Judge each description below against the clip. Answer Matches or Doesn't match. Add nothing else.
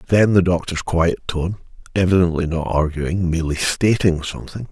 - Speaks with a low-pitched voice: Matches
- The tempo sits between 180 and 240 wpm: Doesn't match